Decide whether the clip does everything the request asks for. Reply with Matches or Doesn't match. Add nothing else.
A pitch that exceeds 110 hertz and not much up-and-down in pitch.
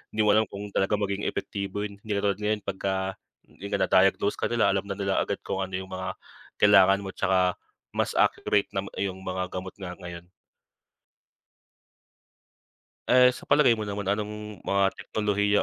Doesn't match